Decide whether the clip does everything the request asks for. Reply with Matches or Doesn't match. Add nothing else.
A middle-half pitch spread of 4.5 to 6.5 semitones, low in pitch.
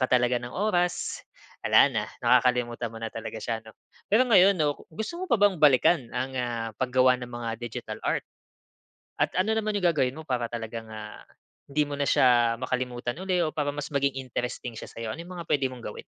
Matches